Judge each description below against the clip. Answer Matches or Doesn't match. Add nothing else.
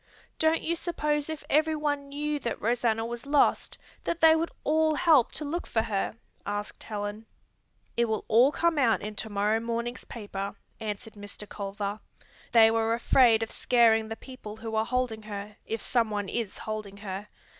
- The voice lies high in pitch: Matches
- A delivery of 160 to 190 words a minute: Matches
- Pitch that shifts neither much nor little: Matches